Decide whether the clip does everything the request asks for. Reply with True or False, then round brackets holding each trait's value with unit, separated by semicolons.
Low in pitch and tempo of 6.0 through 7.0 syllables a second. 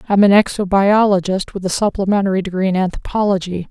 False (195 Hz; 6.3 syllables/s)